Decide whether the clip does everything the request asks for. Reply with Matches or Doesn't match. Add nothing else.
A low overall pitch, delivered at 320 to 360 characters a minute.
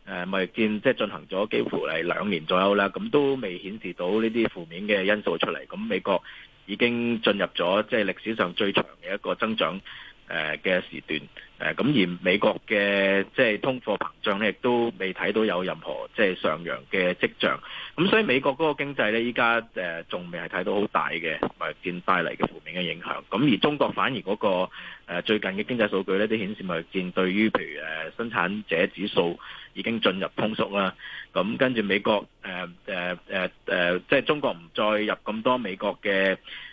Doesn't match